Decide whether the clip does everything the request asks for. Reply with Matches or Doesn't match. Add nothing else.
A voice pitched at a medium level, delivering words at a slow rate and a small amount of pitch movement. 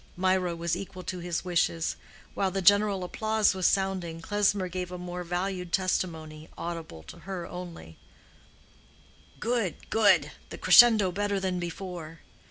Matches